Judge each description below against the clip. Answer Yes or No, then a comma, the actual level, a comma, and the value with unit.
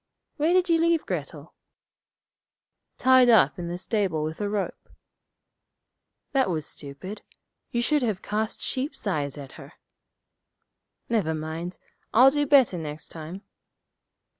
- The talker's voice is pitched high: Yes, high, 205 Hz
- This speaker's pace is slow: Yes, slow, 130 wpm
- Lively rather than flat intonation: Yes, wide, 8.3 semitones